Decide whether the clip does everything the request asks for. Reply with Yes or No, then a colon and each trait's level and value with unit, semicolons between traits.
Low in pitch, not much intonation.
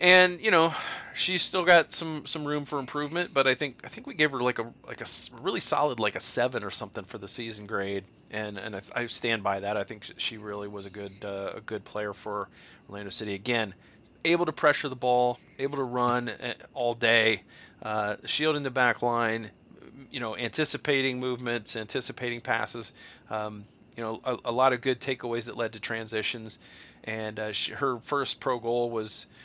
No: low, 120 Hz; average, 3.9 semitones